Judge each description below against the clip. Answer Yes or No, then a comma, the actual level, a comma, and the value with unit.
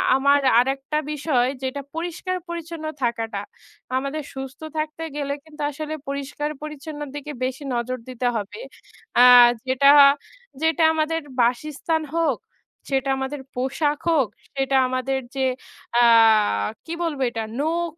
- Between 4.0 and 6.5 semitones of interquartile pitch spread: No, average, 2.9 semitones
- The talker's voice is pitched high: Yes, very high, 280 Hz